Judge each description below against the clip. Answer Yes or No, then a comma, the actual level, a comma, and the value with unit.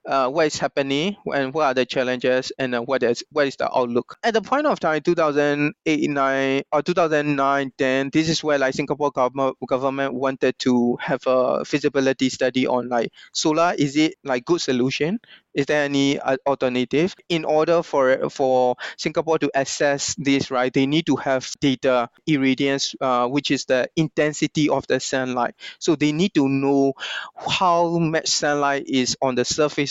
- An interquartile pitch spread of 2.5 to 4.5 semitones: Yes, average, 2.8 semitones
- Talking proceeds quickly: No, average, 175 wpm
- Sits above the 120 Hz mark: Yes, medium, 140 Hz